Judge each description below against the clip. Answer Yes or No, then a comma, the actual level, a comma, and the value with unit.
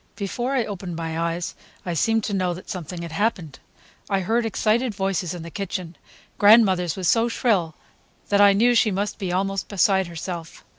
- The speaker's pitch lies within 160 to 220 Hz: Yes, high, 190 Hz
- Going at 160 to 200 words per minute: Yes, average, 180 wpm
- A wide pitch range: No, average, 3.5 semitones